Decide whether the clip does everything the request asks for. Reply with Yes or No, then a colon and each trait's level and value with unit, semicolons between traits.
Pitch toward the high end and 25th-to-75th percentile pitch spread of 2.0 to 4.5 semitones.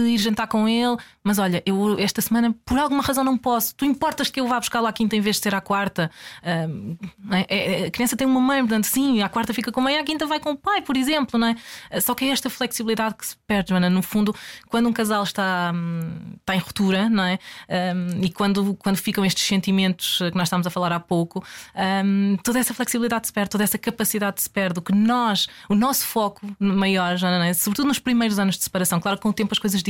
Yes: high, 210 Hz; average, 3.7 semitones